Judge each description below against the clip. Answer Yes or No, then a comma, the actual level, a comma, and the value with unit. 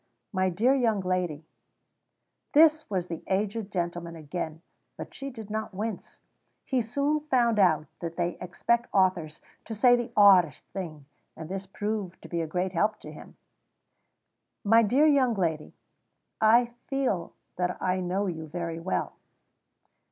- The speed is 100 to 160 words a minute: Yes, average, 150 wpm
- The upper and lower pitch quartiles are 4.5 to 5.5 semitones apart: Yes, average, 4.8 semitones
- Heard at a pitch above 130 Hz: Yes, high, 190 Hz